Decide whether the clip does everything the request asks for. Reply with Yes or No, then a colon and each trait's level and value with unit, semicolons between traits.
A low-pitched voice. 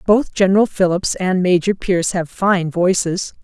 No: medium, 185 Hz